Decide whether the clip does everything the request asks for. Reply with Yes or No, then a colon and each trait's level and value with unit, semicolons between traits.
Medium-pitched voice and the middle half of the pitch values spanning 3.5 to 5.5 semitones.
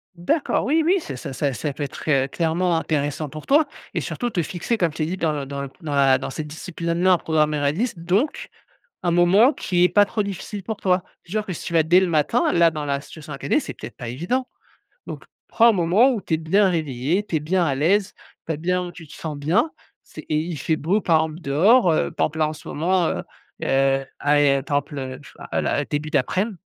Yes: medium, 165 Hz; average, 4.2 semitones